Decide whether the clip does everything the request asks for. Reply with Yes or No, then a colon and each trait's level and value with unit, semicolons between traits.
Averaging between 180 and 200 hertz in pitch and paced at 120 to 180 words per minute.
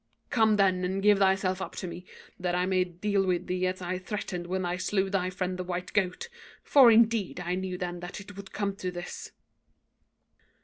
No: medium, 185 Hz; fast, 205 wpm